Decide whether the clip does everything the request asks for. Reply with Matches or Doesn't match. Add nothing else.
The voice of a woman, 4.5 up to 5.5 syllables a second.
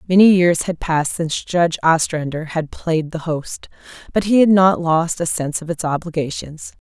Matches